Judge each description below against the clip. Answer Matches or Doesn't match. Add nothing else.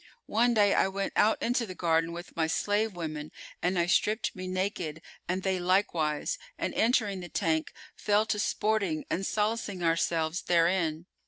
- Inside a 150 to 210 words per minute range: Matches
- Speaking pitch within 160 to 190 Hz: Matches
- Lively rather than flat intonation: Doesn't match